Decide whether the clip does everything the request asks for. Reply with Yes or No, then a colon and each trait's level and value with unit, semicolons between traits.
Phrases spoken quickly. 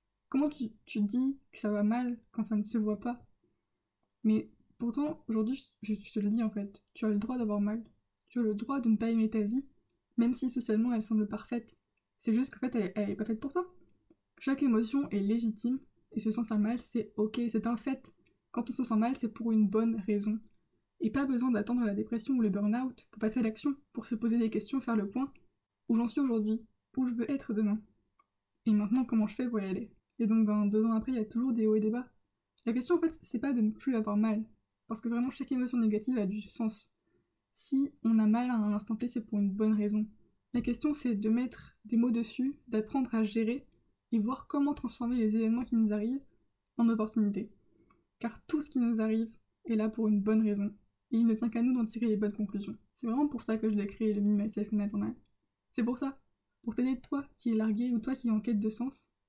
Yes: fast, 245 wpm